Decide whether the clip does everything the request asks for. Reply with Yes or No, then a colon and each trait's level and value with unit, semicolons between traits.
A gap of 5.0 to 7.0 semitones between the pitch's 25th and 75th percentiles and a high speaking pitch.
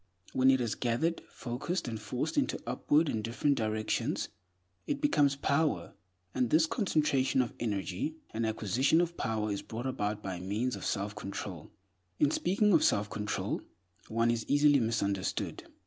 No: wide, 5.4 semitones; low, 120 Hz